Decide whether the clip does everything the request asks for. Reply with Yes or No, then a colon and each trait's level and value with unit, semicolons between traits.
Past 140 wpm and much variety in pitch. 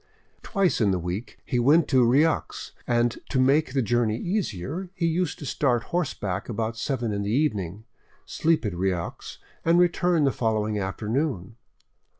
Yes: average, 150 wpm; wide, 6.9 semitones